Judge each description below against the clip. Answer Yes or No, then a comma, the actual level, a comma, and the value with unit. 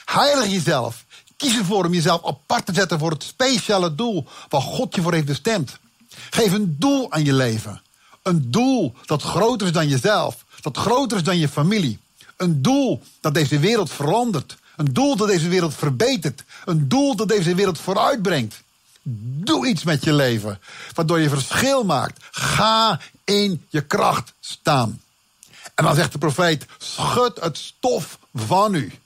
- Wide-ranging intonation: Yes, wide, 6.6 semitones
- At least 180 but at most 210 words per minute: No, average, 165 wpm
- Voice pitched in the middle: Yes, medium, 175 Hz